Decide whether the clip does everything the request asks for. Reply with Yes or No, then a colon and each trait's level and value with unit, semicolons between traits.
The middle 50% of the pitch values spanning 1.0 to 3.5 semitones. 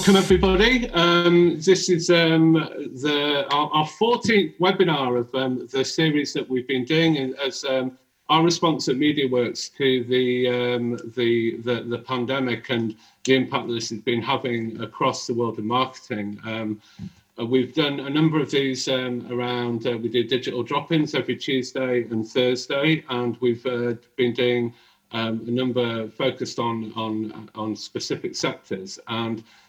No: average, 4.1 semitones